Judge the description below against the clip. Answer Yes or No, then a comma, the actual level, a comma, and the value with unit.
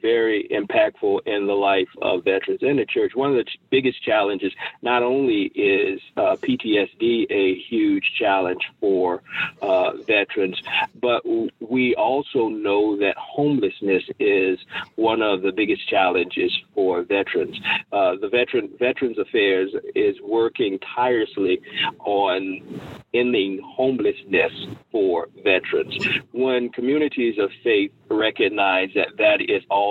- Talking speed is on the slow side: Yes, slow, 130 wpm